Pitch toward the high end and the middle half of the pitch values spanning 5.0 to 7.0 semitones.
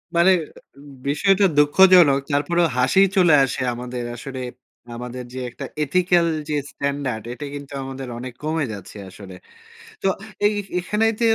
No: medium, 145 Hz; wide, 5.6 semitones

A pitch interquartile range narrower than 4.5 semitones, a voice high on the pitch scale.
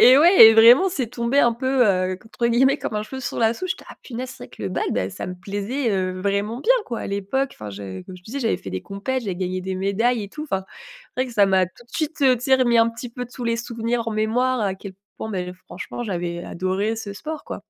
No: average, 4.8 semitones; high, 225 Hz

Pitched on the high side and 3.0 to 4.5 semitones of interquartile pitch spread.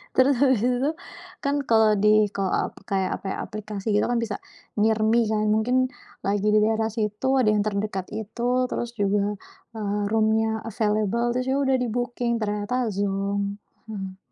No: high, 215 Hz; narrow, 2.5 semitones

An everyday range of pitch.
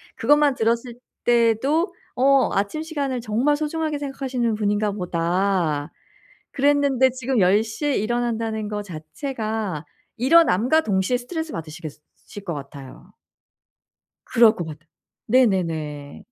No: wide, 6.1 semitones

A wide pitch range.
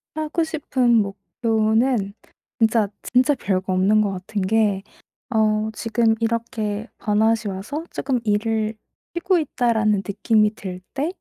No: average, 2.7 semitones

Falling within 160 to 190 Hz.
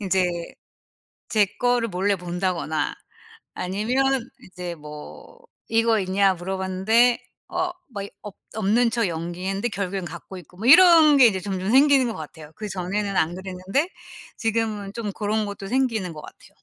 No: high, 200 Hz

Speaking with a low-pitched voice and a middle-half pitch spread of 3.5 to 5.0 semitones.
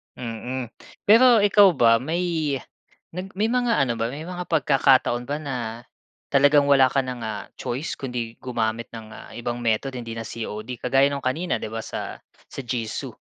Yes: low, 130 Hz; average, 4.7 semitones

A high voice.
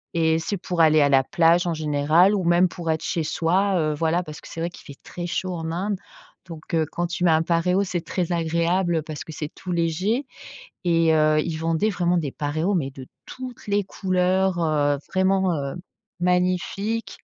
No: medium, 170 Hz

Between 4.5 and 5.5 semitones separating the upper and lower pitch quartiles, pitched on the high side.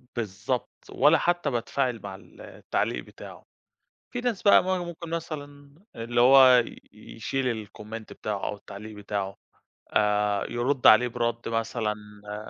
No: average, 4.9 semitones; low, 115 Hz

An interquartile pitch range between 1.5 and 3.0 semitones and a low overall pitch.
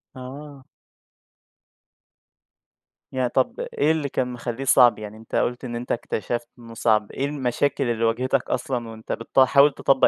Yes: average, 2.7 semitones; low, 125 Hz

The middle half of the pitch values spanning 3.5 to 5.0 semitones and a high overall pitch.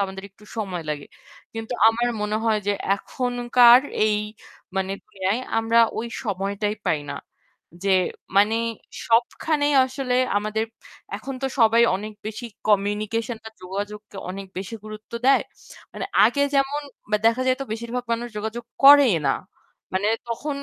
No: average, 3.0 semitones; high, 220 Hz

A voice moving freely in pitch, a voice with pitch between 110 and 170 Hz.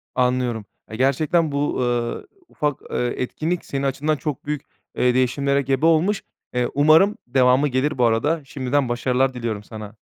No: average, 3.1 semitones; low, 135 Hz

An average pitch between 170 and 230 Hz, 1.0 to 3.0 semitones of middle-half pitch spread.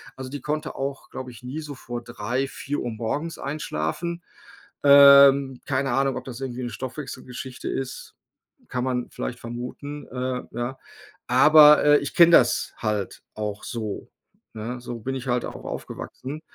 No: low, 130 Hz; narrow, 2.6 semitones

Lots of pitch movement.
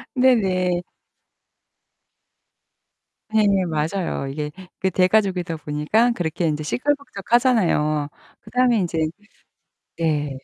Yes: wide, 6.3 semitones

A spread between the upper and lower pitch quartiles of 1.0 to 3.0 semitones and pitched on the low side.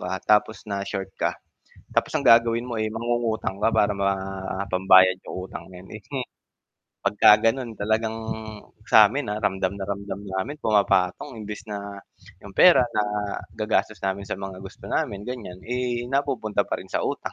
Yes: average, 2.7 semitones; low, 105 Hz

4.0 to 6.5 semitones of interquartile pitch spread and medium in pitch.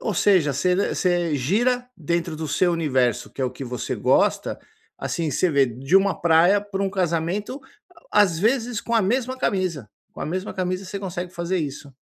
Yes: average, 4.4 semitones; medium, 180 Hz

